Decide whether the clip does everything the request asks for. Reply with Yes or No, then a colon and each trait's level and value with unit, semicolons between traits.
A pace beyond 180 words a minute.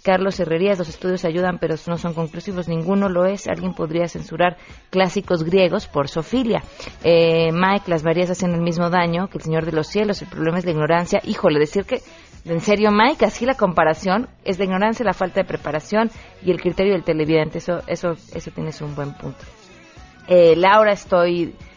Yes: fast, 190 wpm